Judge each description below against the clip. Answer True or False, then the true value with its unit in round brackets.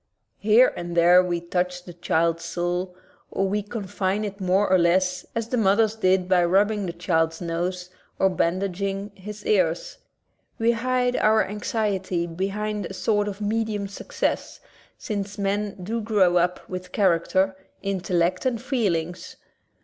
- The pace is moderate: True (145 wpm)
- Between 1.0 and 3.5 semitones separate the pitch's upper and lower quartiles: True (2.9 semitones)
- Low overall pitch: False (190 Hz)